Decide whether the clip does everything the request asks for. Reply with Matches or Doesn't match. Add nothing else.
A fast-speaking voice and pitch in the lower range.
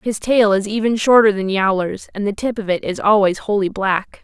Doesn't match